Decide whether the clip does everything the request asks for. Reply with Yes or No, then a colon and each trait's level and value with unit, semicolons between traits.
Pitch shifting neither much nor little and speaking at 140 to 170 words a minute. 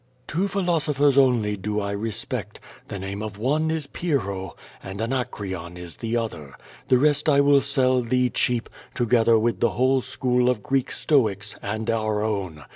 Yes: average, 4.7 semitones; average, 165 wpm